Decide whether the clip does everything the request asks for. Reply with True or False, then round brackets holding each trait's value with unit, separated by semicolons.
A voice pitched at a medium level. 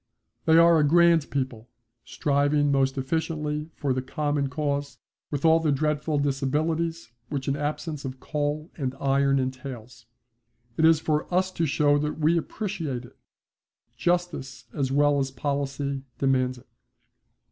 True (145 Hz)